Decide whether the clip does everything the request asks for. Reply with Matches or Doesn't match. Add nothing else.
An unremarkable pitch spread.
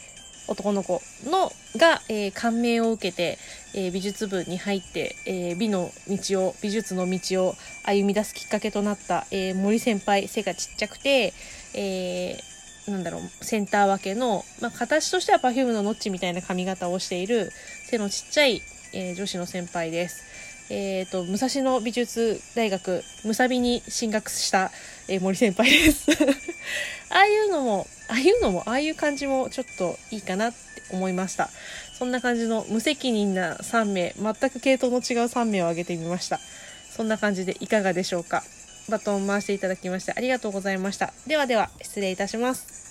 Matches